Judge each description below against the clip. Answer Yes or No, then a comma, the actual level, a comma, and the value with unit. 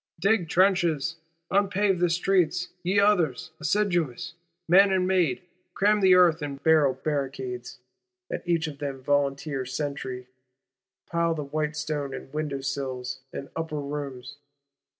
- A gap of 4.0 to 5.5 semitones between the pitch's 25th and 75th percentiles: Yes, average, 4.4 semitones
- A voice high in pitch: No, medium, 155 Hz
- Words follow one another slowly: Yes, slow, 130 wpm